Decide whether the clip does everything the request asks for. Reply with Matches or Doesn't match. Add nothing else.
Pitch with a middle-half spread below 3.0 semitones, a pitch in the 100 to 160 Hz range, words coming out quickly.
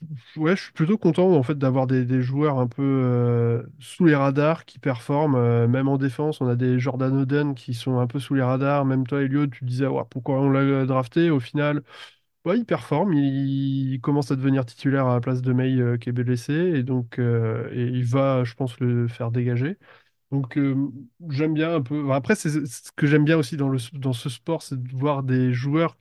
Matches